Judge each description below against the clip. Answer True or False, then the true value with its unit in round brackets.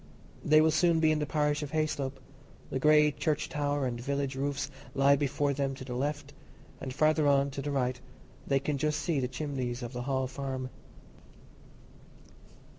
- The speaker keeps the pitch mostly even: True (2.2 semitones)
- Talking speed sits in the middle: True (180 wpm)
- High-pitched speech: False (140 Hz)